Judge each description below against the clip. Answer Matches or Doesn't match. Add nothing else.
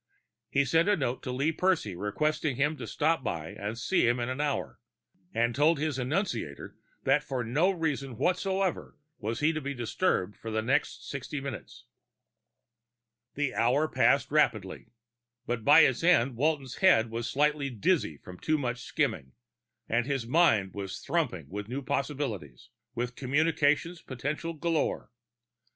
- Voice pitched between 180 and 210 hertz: Doesn't match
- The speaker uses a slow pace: Doesn't match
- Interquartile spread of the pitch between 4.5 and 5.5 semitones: Matches